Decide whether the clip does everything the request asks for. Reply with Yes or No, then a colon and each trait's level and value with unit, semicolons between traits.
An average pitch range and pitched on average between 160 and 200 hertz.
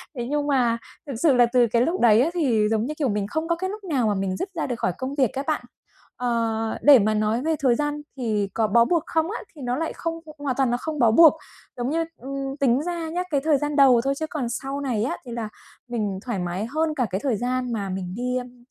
No: average, 4.4 semitones; very high, 255 Hz